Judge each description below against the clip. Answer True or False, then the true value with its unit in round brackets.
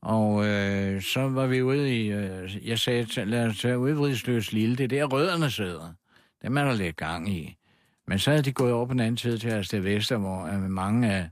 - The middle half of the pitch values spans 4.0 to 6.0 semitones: True (4.3 semitones)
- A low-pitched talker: True (110 Hz)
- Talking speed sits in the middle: False (240 wpm)